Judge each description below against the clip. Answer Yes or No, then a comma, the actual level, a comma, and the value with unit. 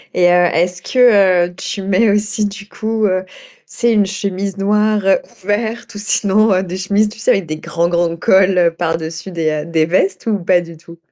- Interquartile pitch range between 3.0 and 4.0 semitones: Yes, average, 3.3 semitones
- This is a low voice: No, high, 190 Hz